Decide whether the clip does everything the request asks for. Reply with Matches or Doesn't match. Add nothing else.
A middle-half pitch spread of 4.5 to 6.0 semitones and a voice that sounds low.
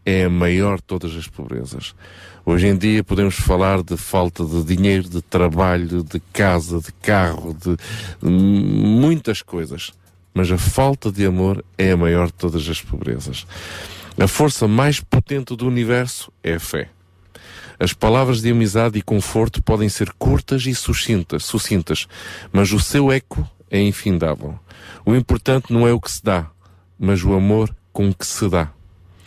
Doesn't match